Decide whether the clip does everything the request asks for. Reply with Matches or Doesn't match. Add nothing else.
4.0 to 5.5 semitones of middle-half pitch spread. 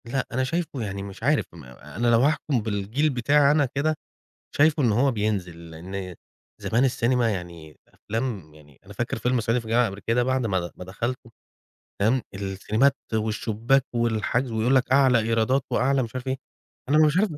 Matches